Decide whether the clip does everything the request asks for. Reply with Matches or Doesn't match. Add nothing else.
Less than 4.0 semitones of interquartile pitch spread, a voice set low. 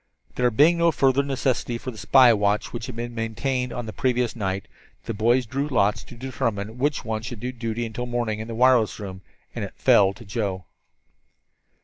Matches